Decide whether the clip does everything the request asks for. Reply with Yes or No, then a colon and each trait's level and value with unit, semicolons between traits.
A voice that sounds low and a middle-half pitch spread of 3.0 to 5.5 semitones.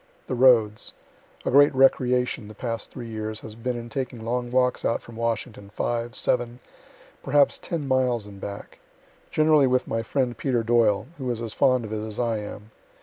No: low, 120 Hz; narrow, 2.6 semitones